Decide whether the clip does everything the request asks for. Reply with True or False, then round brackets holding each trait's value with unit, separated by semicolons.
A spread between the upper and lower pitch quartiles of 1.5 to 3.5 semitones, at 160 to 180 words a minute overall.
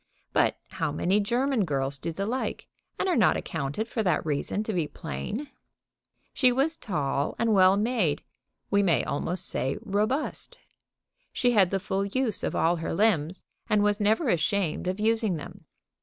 False (5.2 semitones; 170 wpm)